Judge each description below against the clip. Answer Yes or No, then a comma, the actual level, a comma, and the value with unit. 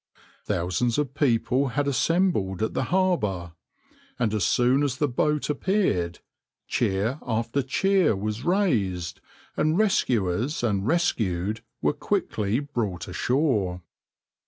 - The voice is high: No, low, 120 Hz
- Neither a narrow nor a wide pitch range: No, wide, 7.1 semitones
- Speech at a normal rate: No, slow, 115 wpm